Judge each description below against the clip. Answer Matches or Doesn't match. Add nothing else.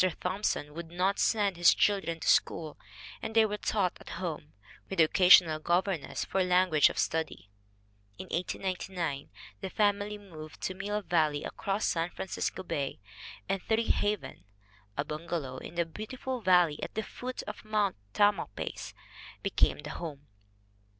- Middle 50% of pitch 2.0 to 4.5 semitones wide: Matches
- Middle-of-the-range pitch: Matches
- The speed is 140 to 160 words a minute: Matches